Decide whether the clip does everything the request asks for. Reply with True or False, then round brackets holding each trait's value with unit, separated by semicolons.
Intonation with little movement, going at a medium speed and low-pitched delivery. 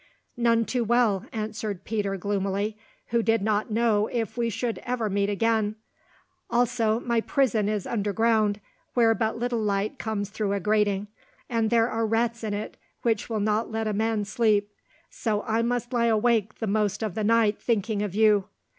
False (1.9 semitones; 175 wpm; 220 Hz)